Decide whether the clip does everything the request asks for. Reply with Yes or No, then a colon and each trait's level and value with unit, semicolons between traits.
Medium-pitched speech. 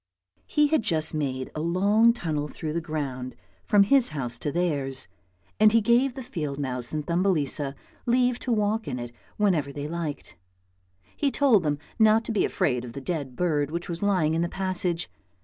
Yes: medium, 170 Hz